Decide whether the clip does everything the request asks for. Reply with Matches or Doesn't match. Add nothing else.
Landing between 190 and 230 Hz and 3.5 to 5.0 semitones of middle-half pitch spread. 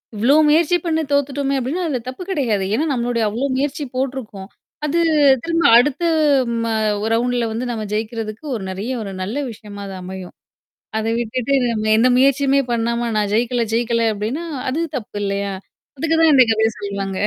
Doesn't match